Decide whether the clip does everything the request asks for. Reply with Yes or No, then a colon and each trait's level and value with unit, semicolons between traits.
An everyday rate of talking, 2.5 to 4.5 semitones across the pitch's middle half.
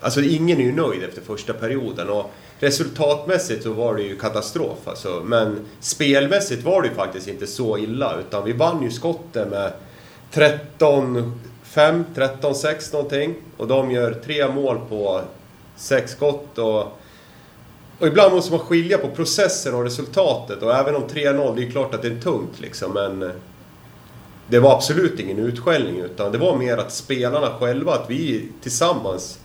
No: average, 165 wpm; average, 5.0 semitones